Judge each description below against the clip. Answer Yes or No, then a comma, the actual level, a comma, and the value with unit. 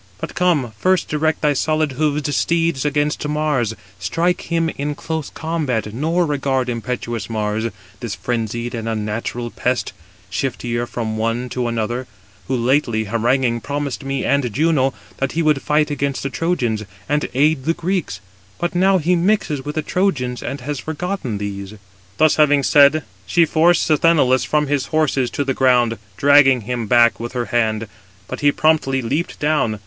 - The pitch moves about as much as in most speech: Yes, average, 4.6 semitones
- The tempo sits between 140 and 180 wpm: Yes, average, 165 wpm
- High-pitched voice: No, low, 135 Hz